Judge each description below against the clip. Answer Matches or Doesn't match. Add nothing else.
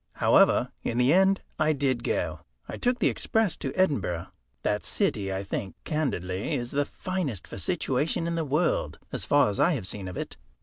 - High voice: Doesn't match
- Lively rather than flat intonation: Matches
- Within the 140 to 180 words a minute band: Doesn't match